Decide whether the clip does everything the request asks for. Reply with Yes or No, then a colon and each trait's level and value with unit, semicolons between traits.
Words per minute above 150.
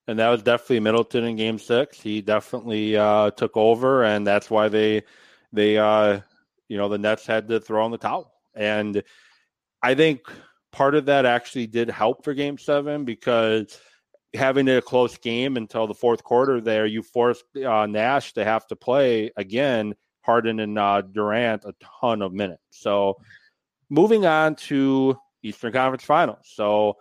Yes: average, 170 wpm